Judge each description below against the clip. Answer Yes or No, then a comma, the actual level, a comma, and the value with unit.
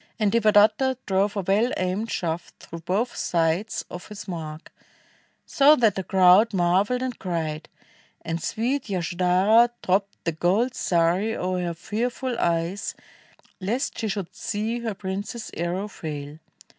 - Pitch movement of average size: Yes, average, 4.3 semitones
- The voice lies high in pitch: Yes, high, 195 Hz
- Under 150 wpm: Yes, average, 140 wpm